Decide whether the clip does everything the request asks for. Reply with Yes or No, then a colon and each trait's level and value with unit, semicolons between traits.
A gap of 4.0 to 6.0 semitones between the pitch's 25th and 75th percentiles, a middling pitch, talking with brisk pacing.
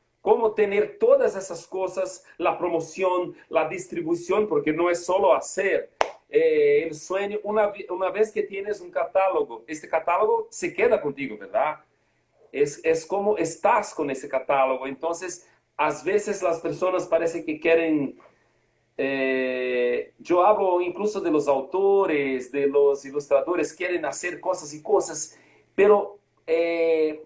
No: average, 5.1 semitones; medium, 180 Hz; average, 135 wpm